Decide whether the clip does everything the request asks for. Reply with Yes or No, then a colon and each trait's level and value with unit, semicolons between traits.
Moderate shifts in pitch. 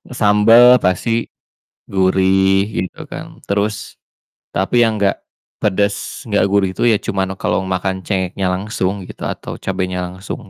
No: narrow, 1.8 semitones